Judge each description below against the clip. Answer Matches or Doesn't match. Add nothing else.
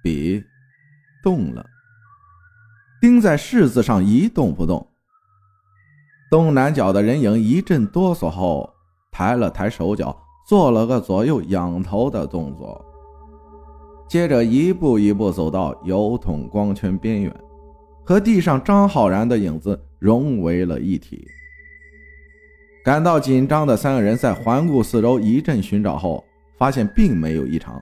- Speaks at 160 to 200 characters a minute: Matches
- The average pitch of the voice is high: Doesn't match